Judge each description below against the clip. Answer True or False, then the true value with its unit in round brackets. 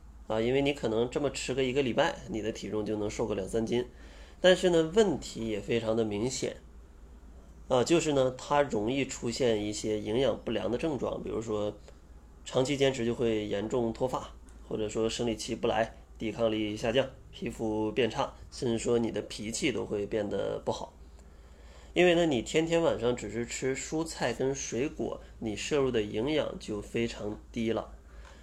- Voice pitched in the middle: False (115 Hz)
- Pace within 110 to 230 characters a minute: False (260 characters per minute)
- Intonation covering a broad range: False (4.0 semitones)